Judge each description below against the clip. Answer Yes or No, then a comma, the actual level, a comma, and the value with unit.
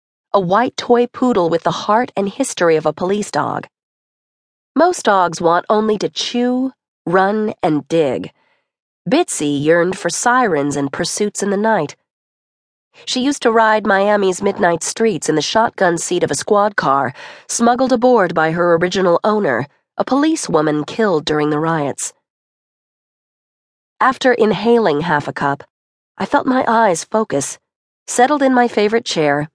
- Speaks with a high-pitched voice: Yes, high, 200 Hz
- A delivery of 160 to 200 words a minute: No, average, 150 wpm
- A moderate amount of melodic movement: No, wide, 6.3 semitones